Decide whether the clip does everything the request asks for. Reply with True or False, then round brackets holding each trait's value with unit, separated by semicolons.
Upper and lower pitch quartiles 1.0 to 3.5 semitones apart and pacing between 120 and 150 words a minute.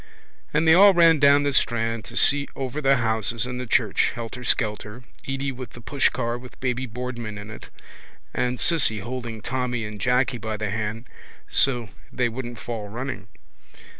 False (2.9 semitones; 165 wpm)